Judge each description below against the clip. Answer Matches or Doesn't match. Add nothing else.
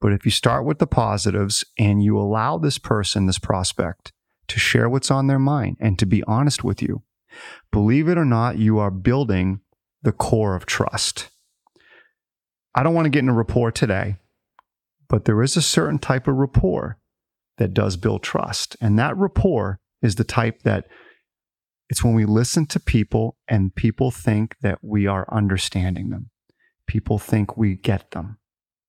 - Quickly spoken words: Doesn't match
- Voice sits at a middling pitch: Doesn't match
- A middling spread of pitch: Matches